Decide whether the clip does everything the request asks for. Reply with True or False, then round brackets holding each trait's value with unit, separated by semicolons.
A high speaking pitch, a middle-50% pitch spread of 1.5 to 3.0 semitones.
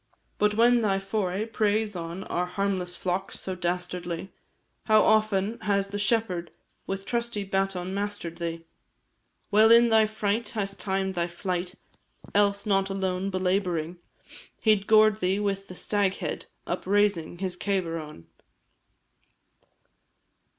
True (195 Hz; 2.5 semitones)